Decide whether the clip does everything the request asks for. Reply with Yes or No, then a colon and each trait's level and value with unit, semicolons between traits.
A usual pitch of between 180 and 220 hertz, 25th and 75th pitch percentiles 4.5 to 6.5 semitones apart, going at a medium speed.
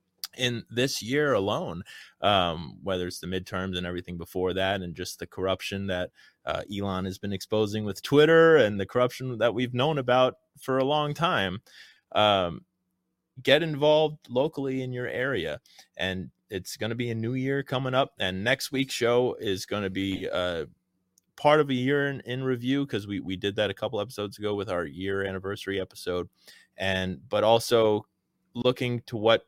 No: low, 115 Hz; wide, 5.6 semitones; average, 180 wpm